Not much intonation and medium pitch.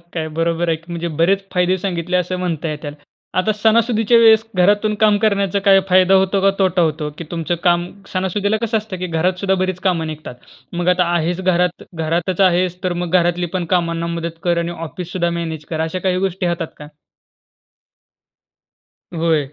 Yes: narrow, 2.3 semitones; medium, 180 Hz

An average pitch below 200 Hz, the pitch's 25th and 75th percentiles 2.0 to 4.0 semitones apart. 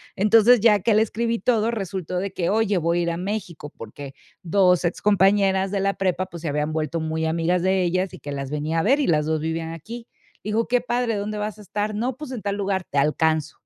No: high, 190 Hz; average, 4.5 semitones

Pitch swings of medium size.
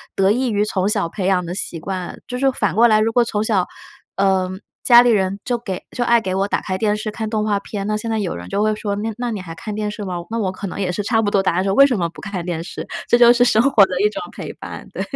Yes: average, 3.0 semitones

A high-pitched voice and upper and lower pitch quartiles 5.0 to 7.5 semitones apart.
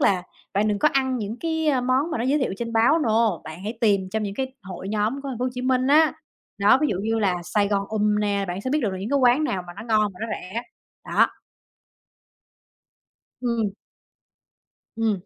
No: high, 225 Hz; average, 4.3 semitones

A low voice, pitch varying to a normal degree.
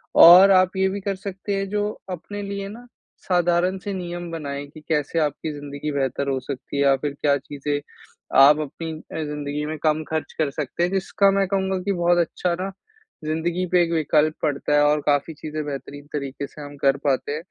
No: medium, 155 Hz; average, 4.2 semitones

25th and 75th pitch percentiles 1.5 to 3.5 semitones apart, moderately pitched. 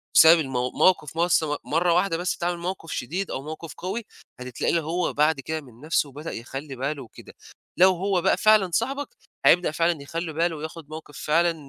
Yes: average, 3.1 semitones; medium, 165 Hz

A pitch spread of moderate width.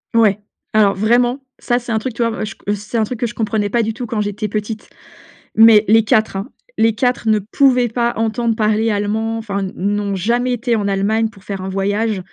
No: narrow, 2.2 semitones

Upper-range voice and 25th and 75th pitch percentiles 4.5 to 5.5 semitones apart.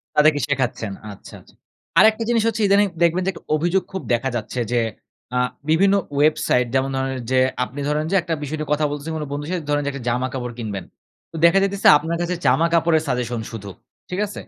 No: medium, 150 Hz; average, 5.0 semitones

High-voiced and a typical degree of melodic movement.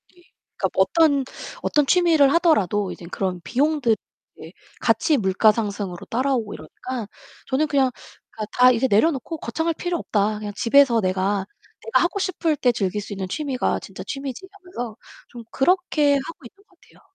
No: very high, 260 Hz; wide, 7.0 semitones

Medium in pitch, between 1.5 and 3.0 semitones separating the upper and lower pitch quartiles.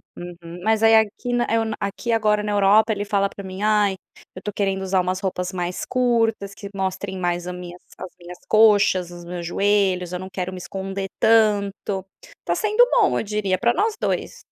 No: high, 200 Hz; average, 2.7 semitones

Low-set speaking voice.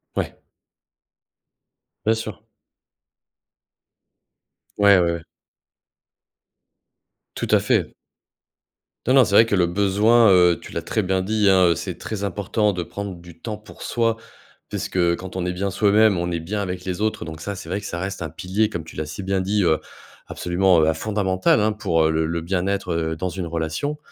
Yes: very low, 95 Hz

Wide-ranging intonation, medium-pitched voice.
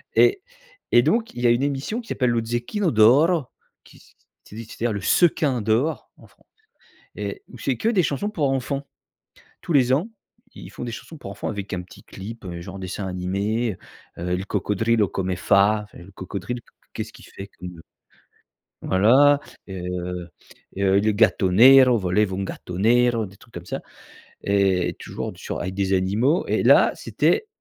No: wide, 5.7 semitones; low, 110 Hz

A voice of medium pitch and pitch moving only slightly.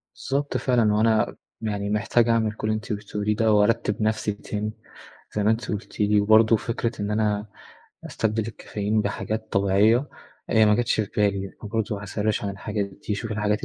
No: low, 105 Hz; narrow, 1.3 semitones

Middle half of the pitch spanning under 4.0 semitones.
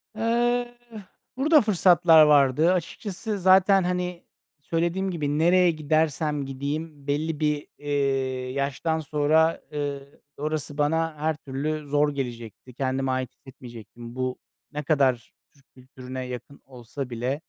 Yes: average, 3.6 semitones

